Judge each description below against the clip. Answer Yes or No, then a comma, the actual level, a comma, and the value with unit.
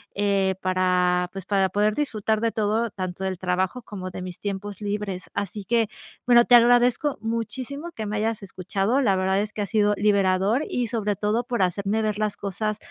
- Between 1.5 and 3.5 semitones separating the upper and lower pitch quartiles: Yes, average, 2.8 semitones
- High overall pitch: Yes, high, 205 Hz